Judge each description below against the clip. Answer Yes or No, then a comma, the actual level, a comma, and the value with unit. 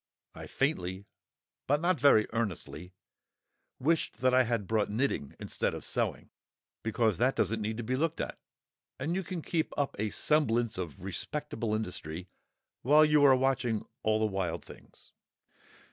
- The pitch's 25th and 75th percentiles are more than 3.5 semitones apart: Yes, wide, 5.4 semitones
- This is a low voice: Yes, low, 115 Hz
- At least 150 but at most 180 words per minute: Yes, average, 155 wpm